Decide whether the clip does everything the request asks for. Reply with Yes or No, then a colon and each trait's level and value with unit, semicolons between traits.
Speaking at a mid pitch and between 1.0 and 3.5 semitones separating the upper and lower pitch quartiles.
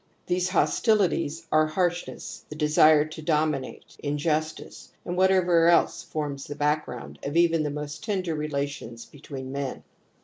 Yes: medium, 155 Hz; average, 2.7 semitones